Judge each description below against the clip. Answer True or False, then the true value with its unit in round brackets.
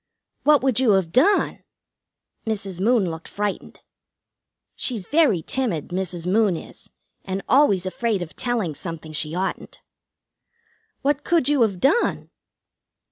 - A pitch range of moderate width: False (6.3 semitones)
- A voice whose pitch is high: True (200 Hz)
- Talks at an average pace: False (130 wpm)